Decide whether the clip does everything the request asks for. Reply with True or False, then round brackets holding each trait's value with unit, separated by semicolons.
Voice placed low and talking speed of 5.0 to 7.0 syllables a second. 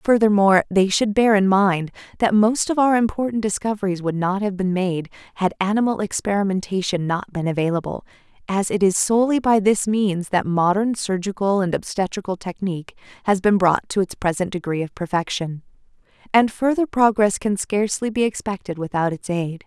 False (195 Hz; 5.4 syllables/s)